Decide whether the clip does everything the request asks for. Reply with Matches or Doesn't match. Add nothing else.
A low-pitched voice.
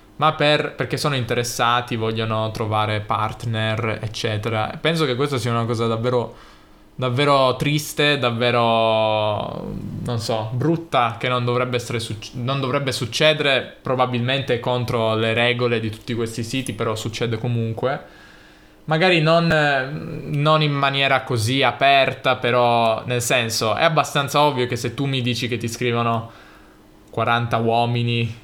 Matches